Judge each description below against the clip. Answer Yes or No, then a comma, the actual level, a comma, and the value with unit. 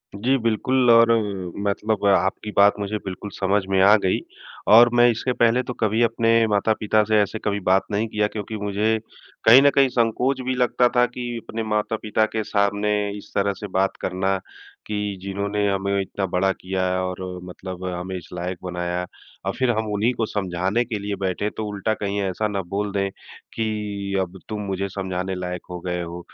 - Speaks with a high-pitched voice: No, low, 100 Hz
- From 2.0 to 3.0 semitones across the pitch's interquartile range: Yes, narrow, 2.6 semitones